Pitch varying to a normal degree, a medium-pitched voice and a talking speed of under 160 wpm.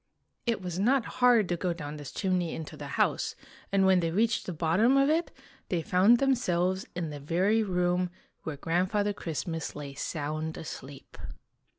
No: average, 4.3 semitones; medium, 180 Hz; average, 170 wpm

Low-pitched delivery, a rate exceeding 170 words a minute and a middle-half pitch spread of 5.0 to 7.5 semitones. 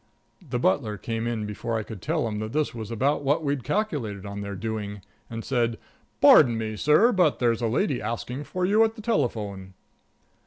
Yes: low, 115 Hz; average, 195 wpm; average, 5.3 semitones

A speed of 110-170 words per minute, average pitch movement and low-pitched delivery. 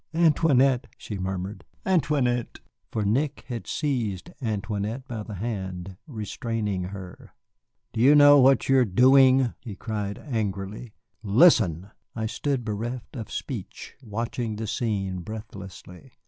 Yes: slow, 135 wpm; average, 4.5 semitones; low, 110 Hz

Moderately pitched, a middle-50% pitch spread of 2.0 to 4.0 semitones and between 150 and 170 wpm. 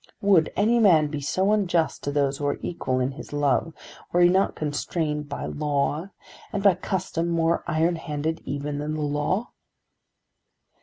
Yes: medium, 155 Hz; average, 3.4 semitones; average, 165 wpm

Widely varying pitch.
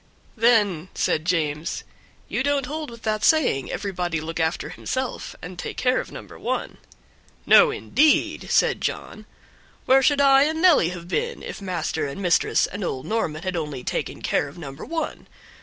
Yes: wide, 8.7 semitones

